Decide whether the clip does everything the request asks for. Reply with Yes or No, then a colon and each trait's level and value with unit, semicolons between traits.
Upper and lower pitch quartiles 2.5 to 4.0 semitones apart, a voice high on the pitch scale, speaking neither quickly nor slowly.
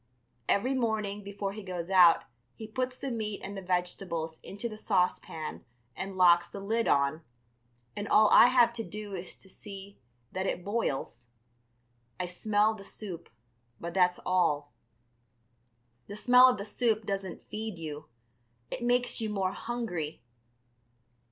Yes: average, 3.5 semitones; high, 200 Hz; average, 150 wpm